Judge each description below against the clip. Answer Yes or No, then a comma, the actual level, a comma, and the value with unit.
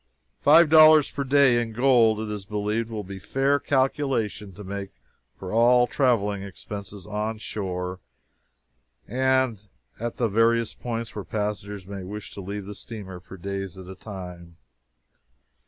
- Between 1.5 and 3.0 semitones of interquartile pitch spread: No, average, 3.7 semitones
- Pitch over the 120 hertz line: No, low, 105 Hz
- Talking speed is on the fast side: No, average, 150 wpm